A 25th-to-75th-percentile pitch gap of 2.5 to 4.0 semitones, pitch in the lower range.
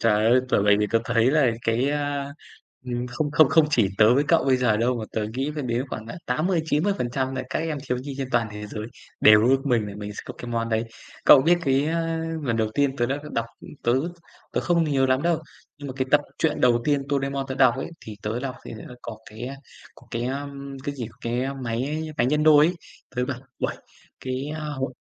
Yes: average, 3.5 semitones; low, 130 Hz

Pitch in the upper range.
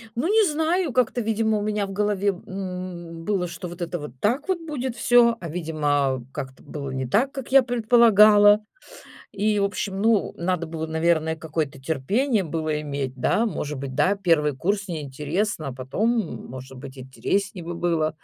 No: medium, 180 Hz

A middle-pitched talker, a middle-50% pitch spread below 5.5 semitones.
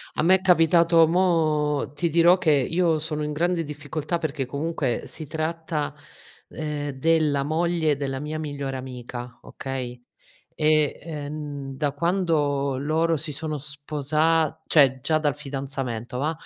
Yes: medium, 150 Hz; average, 2.7 semitones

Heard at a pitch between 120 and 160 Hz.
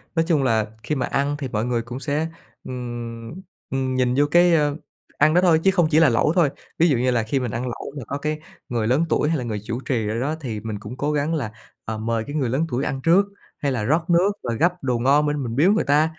Yes: low, 135 Hz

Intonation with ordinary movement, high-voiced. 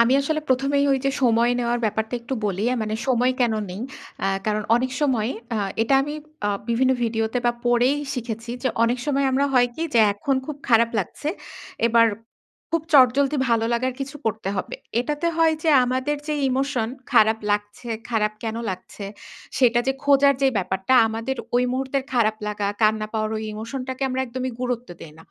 Yes: average, 3.3 semitones; high, 245 Hz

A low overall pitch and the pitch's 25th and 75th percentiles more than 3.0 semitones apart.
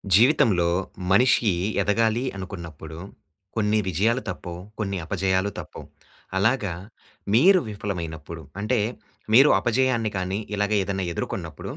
Yes: low, 100 Hz; average, 4.0 semitones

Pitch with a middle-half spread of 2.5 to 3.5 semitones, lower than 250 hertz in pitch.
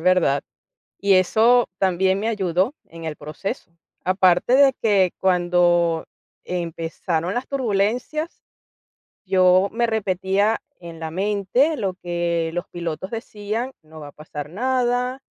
No: average, 4.5 semitones; high, 190 Hz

